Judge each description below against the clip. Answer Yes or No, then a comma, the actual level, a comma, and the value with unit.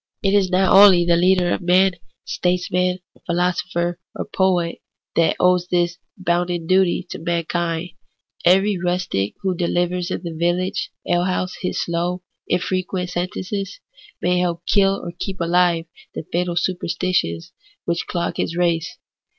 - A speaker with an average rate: Yes, average, 145 wpm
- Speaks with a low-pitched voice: No, medium, 180 Hz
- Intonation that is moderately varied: No, narrow, 1.2 semitones